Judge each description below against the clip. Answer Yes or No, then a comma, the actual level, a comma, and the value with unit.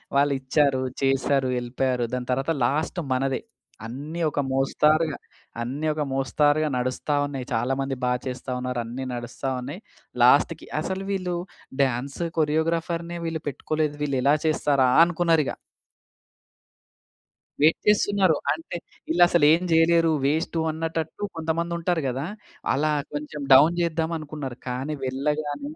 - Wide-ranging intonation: No, average, 3.5 semitones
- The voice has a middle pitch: Yes, medium, 150 Hz